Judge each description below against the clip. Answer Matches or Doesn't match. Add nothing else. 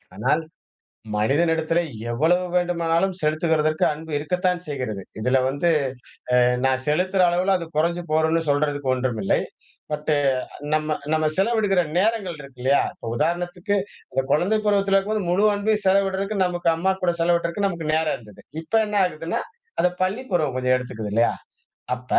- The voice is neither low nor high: Matches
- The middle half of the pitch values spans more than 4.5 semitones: Doesn't match